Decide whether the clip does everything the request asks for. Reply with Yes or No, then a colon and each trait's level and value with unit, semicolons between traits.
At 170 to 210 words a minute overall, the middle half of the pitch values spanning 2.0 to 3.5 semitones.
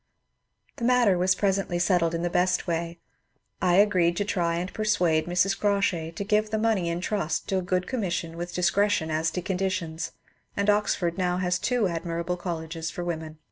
Yes: average, 185 wpm; average, 2.9 semitones